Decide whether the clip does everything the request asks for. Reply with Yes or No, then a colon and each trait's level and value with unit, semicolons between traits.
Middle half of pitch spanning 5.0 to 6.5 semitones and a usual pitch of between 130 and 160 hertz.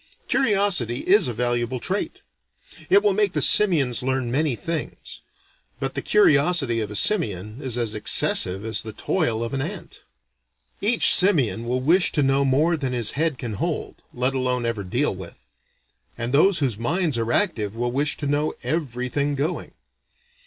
Yes: wide, 5.5 semitones; low, 135 Hz